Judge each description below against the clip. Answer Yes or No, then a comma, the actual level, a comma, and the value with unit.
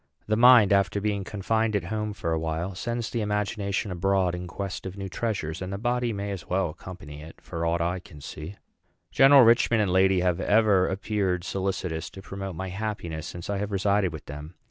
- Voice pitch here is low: Yes, very low, 95 Hz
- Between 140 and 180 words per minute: No, fast, 205 wpm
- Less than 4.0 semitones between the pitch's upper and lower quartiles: Yes, average, 2.9 semitones